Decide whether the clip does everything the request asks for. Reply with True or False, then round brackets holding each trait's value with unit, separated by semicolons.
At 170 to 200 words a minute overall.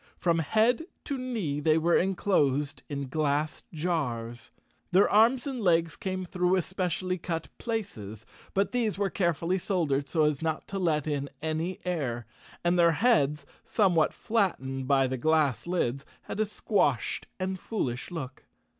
False (150 wpm)